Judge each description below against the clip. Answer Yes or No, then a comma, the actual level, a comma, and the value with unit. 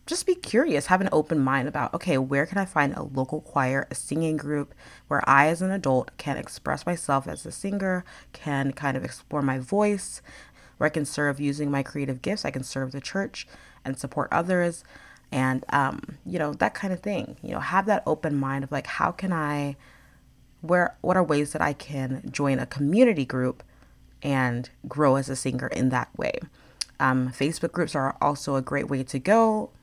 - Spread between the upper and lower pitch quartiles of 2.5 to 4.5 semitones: Yes, average, 4.1 semitones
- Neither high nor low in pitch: Yes, medium, 145 Hz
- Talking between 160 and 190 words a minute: No, average, 200 wpm